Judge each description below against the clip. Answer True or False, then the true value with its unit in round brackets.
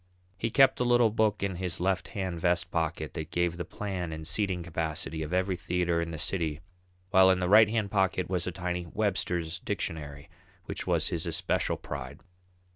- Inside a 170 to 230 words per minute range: True (190 wpm)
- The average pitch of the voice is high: False (90 Hz)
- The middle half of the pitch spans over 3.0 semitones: False (2.7 semitones)